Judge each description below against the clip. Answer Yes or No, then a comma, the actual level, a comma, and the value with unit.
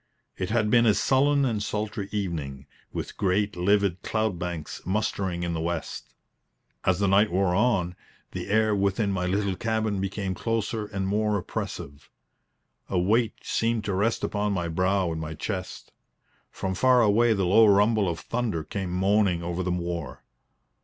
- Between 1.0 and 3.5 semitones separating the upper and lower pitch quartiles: Yes, average, 3.2 semitones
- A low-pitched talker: Yes, low, 100 Hz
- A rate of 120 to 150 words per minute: No, average, 165 wpm